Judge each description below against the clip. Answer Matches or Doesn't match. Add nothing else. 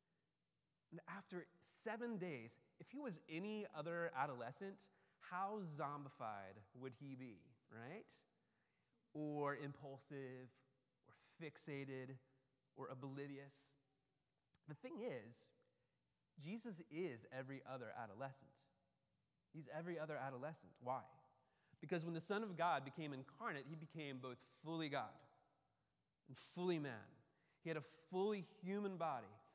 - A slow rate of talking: Matches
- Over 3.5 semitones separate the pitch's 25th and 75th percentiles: Matches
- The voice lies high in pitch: Doesn't match